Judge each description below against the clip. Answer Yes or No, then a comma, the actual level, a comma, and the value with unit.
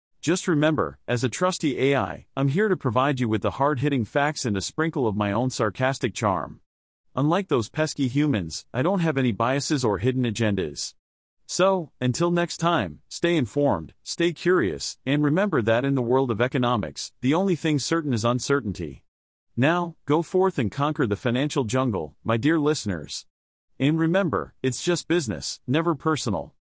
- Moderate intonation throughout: No, wide, 6.3 semitones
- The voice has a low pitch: Yes, low, 130 Hz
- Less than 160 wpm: No, average, 170 wpm